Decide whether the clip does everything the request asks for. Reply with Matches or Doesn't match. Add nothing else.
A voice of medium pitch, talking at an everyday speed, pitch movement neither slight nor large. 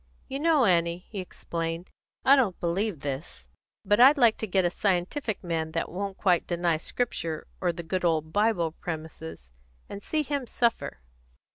Matches